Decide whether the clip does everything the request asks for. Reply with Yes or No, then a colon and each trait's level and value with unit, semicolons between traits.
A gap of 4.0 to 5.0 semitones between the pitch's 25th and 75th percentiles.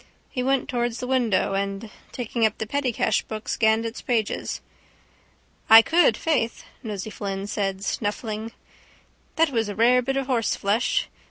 No: average, 3.2 semitones